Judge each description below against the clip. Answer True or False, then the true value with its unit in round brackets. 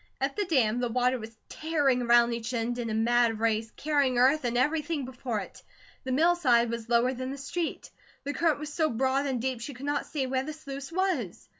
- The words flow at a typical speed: False (225 wpm)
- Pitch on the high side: True (260 Hz)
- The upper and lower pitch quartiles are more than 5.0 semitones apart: False (3.6 semitones)